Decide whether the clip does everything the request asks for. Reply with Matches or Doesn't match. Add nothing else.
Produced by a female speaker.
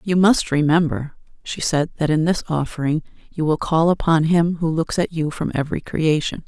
Matches